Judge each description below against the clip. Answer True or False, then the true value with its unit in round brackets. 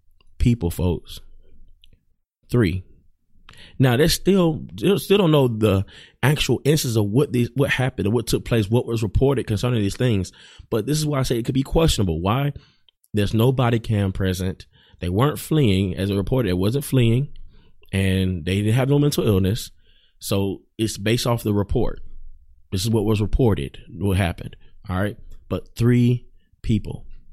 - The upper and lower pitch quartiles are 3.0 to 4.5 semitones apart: False (5.6 semitones)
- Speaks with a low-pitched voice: True (110 Hz)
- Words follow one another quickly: False (170 wpm)